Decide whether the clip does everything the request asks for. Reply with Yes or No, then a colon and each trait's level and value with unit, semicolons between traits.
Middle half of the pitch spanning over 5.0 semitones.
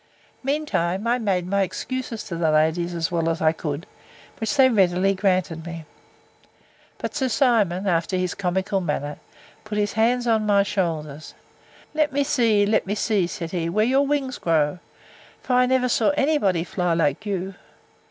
Yes: wide, 5.4 semitones